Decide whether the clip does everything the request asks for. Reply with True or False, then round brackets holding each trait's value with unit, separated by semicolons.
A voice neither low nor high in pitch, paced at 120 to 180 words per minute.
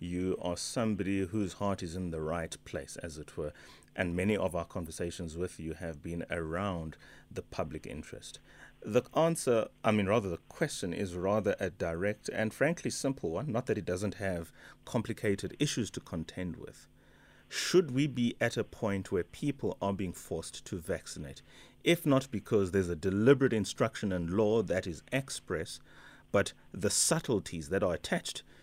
False (100 Hz; 175 wpm)